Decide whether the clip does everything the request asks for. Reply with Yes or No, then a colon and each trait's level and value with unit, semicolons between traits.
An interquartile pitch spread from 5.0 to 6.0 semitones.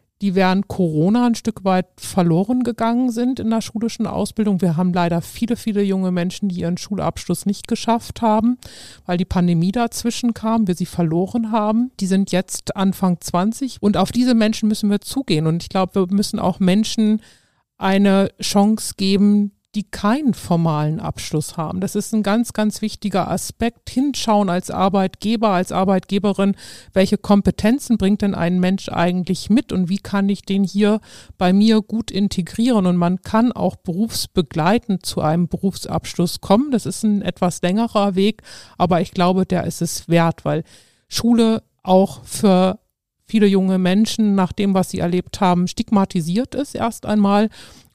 No: average, 3.2 semitones